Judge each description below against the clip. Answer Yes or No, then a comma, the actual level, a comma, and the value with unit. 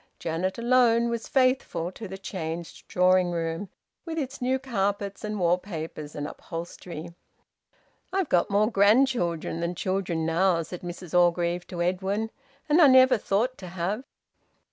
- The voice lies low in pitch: No, high, 190 Hz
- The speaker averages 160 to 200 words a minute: No, average, 145 wpm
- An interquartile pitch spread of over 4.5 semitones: Yes, average, 5.2 semitones